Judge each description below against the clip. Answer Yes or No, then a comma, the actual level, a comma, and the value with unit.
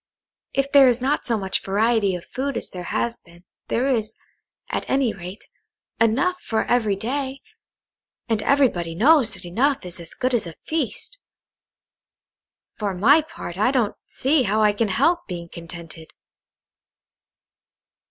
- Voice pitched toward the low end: No, high, 225 Hz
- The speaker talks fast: No, average, 150 wpm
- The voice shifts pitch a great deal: Yes, wide, 6.0 semitones